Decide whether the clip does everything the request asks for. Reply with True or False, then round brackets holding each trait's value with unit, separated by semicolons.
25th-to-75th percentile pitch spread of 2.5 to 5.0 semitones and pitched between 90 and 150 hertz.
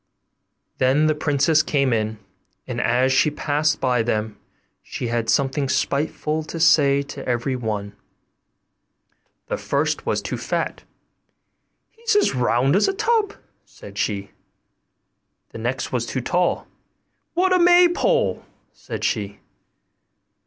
False (5.5 semitones; 140 Hz)